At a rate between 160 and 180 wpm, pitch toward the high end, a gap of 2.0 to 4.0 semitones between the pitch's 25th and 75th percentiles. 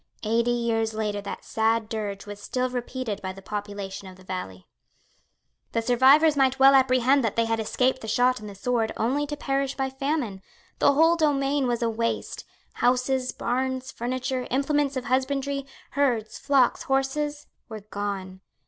Yes: average, 165 wpm; very high, 250 Hz; average, 3.6 semitones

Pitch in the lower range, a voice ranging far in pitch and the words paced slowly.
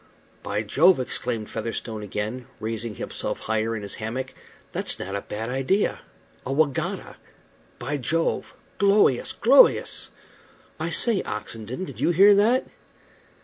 Yes: low, 125 Hz; wide, 7.8 semitones; slow, 130 wpm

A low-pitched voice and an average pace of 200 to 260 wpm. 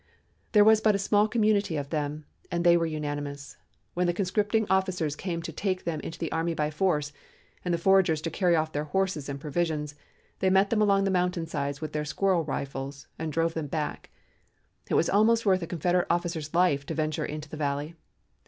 No: medium, 165 Hz; fast, 205 wpm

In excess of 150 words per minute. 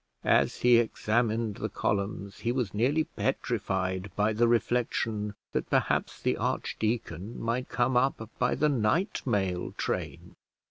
No: slow, 135 wpm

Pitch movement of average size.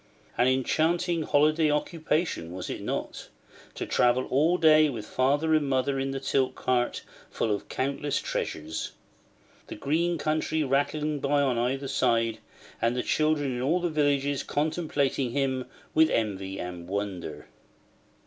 Yes: average, 4.0 semitones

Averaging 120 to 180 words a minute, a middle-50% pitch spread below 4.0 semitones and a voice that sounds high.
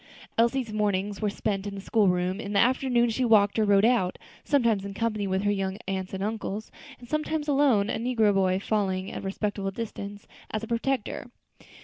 No: average, 200 wpm; average, 2.9 semitones; high, 210 Hz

